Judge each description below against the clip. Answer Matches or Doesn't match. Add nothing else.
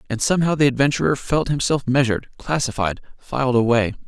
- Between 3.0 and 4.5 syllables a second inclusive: Doesn't match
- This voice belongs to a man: Matches